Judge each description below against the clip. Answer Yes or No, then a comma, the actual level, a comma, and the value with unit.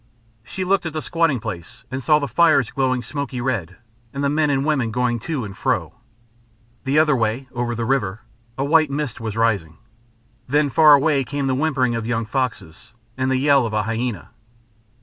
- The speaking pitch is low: Yes, low, 130 Hz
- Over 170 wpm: Yes, average, 190 wpm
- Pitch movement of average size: Yes, average, 4.0 semitones